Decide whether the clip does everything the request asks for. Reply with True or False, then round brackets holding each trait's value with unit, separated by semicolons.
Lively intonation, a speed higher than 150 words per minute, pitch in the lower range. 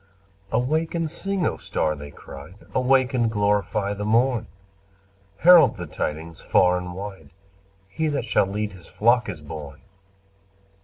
False (6.4 semitones; 145 wpm; 105 Hz)